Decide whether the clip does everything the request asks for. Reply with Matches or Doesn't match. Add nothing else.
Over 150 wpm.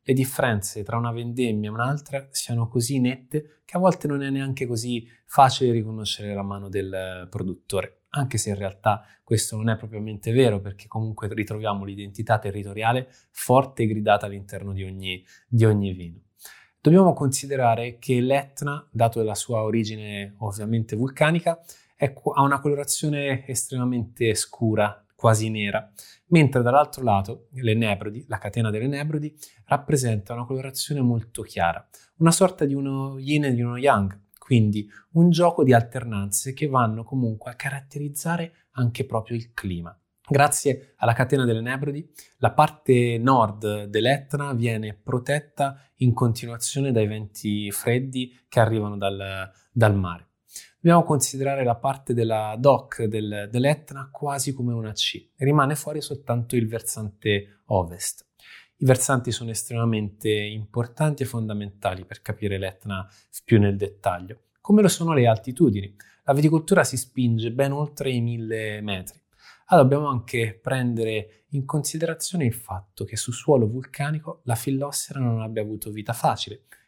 Doesn't match